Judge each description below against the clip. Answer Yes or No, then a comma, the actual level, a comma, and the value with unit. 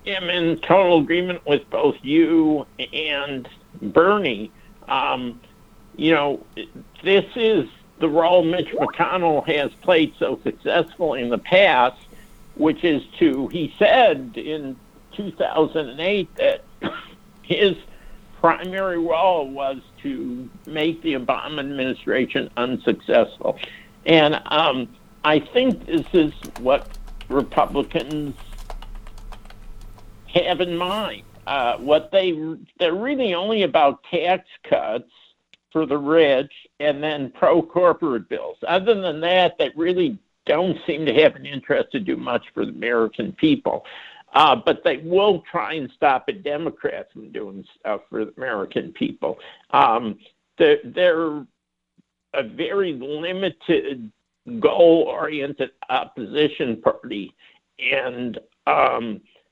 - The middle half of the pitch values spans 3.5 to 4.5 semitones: No, wide, 5.5 semitones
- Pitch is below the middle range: No, medium, 165 Hz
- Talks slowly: Yes, slow, 115 wpm